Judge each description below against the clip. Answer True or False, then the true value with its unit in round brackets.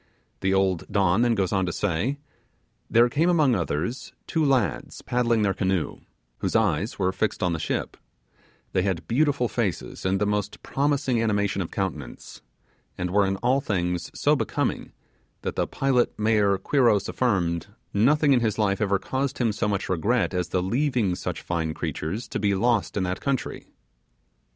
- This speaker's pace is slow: False (170 wpm)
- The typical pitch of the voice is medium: False (105 Hz)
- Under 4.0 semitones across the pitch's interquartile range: False (4.6 semitones)